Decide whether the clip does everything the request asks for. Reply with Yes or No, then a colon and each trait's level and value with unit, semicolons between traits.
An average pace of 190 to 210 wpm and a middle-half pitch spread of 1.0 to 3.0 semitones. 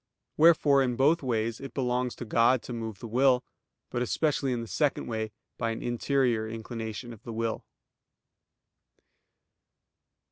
No: average, 145 wpm; average, 2.7 semitones